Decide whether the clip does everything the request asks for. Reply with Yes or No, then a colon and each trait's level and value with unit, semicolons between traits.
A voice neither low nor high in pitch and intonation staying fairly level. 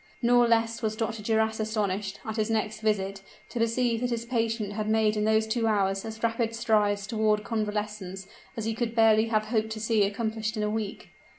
No: high, 220 Hz; narrow, 1.2 semitones